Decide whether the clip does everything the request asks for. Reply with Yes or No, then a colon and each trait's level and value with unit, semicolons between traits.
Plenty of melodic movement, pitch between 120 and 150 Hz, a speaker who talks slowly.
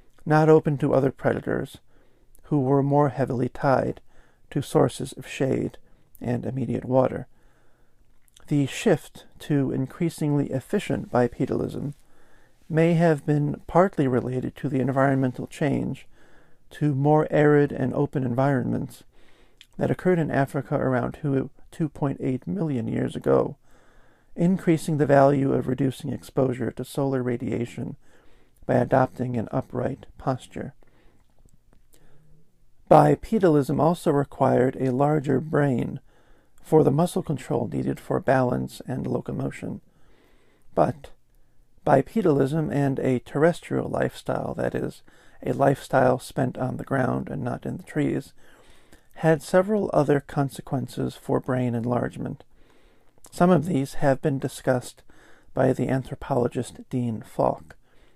No: average, 3.2 semitones; low, 135 Hz; slow, 120 wpm